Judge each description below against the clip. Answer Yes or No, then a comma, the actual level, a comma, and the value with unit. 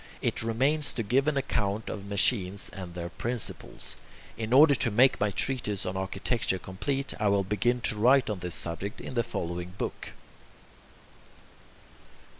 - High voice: No, low, 105 Hz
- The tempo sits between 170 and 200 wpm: No, average, 155 wpm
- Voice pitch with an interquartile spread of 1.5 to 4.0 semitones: No, average, 4.8 semitones